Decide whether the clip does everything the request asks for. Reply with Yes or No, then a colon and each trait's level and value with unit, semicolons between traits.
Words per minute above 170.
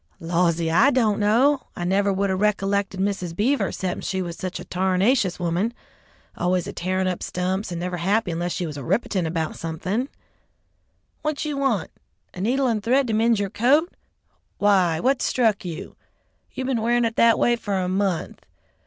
Yes: average, 180 wpm